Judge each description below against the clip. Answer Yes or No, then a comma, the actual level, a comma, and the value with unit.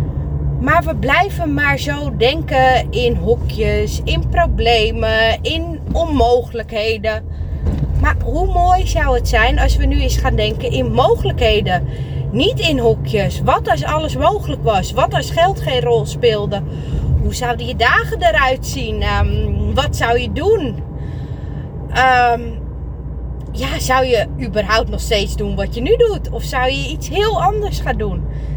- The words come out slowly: No, average, 150 wpm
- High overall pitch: Yes, high, 230 Hz